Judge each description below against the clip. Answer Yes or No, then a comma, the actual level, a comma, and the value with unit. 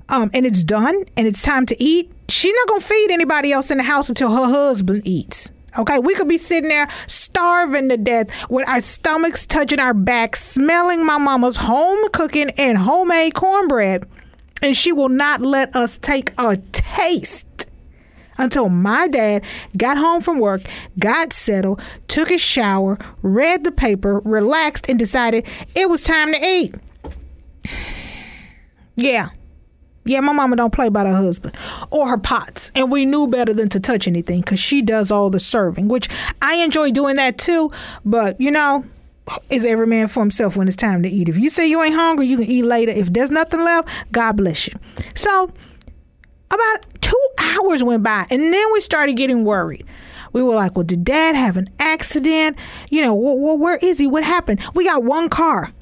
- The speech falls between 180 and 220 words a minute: Yes, average, 185 wpm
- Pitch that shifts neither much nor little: No, wide, 6.6 semitones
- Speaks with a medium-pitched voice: No, very high, 260 Hz